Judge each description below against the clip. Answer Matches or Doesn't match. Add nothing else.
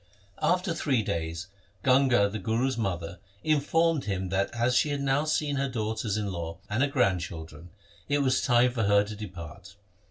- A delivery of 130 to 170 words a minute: Doesn't match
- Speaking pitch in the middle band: Doesn't match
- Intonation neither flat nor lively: Doesn't match